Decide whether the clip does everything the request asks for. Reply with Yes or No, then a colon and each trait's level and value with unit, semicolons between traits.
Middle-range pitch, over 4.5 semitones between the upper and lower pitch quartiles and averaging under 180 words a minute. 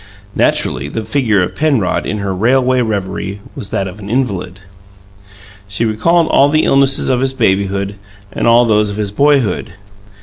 No: low, 110 Hz; average, 5.0 semitones; average, 165 wpm